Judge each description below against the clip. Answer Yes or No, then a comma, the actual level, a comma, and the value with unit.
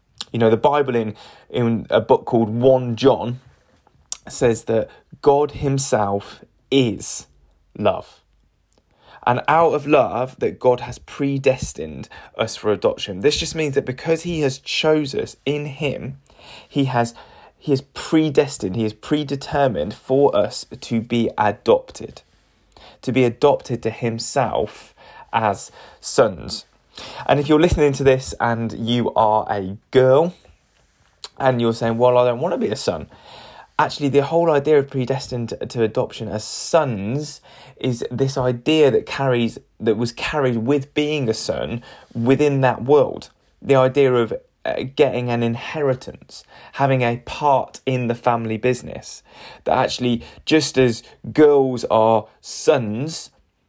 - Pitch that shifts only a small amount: No, average, 3.4 semitones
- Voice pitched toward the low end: Yes, low, 130 Hz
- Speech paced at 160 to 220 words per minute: No, average, 140 wpm